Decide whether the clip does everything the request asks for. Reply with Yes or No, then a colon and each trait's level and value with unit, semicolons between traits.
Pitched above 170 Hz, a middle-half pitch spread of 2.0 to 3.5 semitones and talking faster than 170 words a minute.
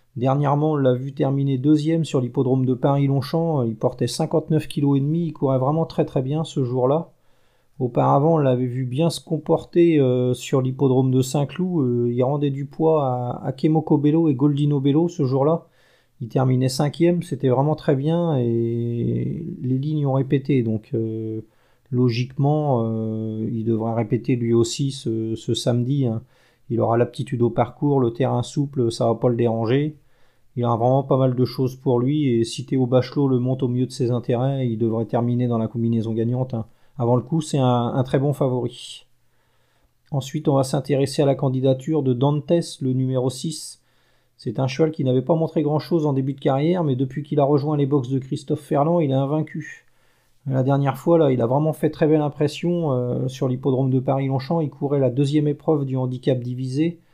No: low, 135 Hz; average, 3.1 semitones; average, 195 wpm